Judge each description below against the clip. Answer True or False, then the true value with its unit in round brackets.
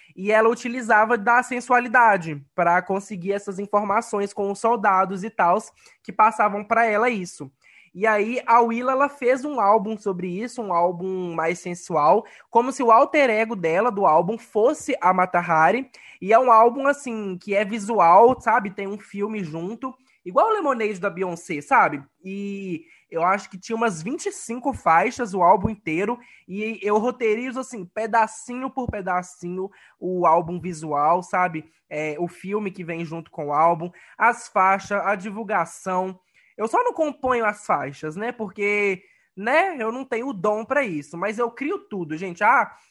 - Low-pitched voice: False (205 Hz)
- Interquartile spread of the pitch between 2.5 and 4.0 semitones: False (4.4 semitones)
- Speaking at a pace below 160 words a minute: False (170 wpm)